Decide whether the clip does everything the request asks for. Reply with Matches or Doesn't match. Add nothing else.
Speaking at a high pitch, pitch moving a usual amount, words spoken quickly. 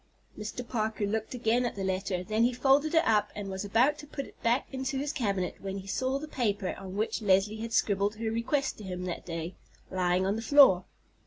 Matches